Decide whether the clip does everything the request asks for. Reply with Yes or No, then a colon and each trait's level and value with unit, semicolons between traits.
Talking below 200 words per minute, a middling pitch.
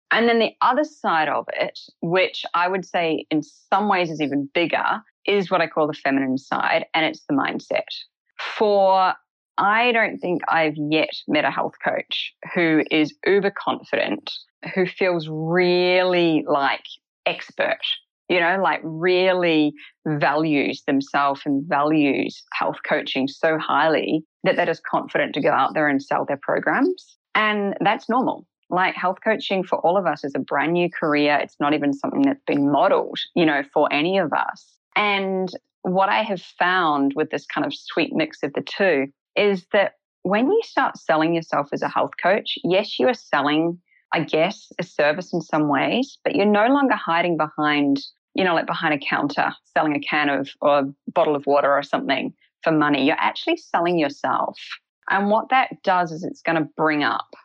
Yes: average, 180 wpm; medium, 170 Hz